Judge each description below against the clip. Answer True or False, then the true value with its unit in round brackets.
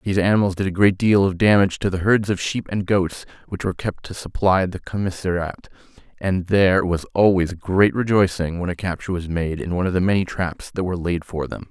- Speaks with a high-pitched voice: False (95 Hz)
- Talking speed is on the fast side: True (225 wpm)